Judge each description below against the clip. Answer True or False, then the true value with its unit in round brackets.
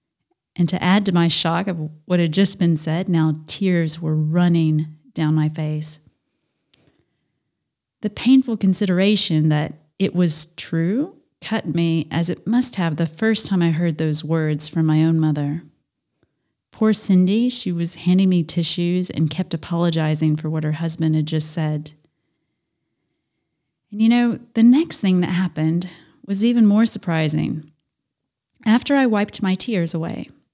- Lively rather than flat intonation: False (3.8 semitones)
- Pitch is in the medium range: True (170 Hz)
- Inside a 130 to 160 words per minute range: True (155 wpm)